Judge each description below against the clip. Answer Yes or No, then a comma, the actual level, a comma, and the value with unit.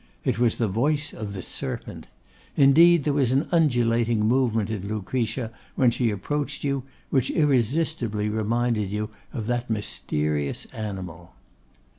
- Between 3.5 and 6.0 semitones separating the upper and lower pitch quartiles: Yes, average, 4.3 semitones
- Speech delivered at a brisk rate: No, slow, 135 wpm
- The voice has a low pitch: Yes, low, 115 Hz